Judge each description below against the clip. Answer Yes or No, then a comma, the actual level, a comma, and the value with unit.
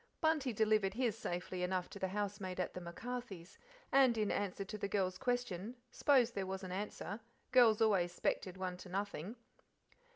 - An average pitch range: Yes, average, 3.6 semitones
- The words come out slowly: No, average, 170 wpm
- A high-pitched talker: Yes, high, 200 Hz